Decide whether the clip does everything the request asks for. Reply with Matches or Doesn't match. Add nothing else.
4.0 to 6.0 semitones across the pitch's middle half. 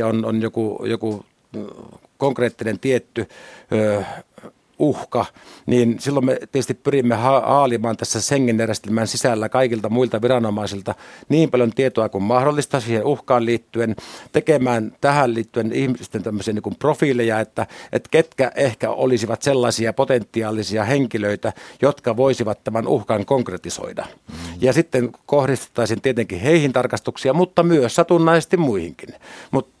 Doesn't match